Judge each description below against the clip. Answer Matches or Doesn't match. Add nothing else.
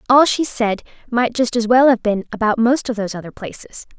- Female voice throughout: Matches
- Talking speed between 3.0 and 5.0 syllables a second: Doesn't match